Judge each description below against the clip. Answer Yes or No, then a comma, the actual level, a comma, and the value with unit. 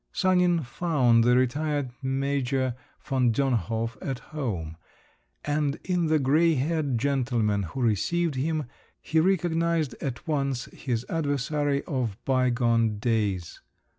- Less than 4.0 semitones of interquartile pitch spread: No, average, 4.4 semitones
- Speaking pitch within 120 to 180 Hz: Yes, low, 135 Hz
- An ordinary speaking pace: No, slow, 115 wpm